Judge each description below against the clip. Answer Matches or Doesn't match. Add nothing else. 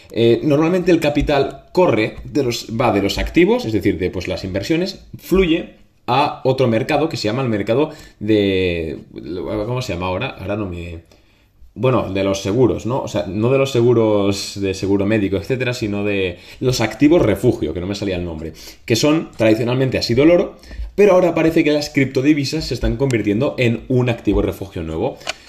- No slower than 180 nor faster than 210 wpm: Matches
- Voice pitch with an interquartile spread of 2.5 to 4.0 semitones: Doesn't match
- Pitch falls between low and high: Doesn't match